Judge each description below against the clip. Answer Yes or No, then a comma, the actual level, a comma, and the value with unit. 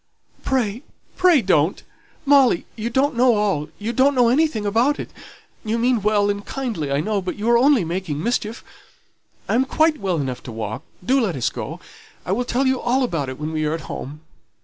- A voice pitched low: No, high, 215 Hz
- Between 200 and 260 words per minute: Yes, fast, 205 wpm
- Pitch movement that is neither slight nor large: No, wide, 7.3 semitones